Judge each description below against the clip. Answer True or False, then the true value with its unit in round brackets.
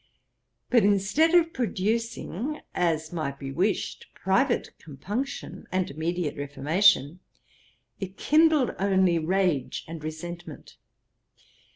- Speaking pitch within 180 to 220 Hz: True (185 Hz)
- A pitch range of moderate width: False (6.2 semitones)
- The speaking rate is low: True (95 wpm)